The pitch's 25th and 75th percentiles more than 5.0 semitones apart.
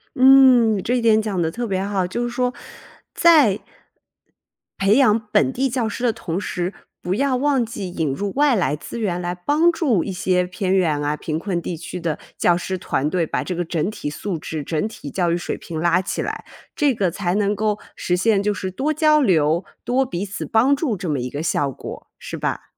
Yes: wide, 5.5 semitones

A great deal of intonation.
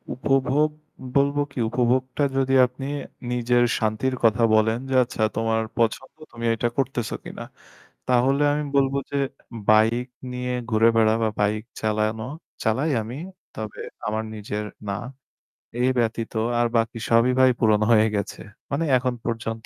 No: average, 2.8 semitones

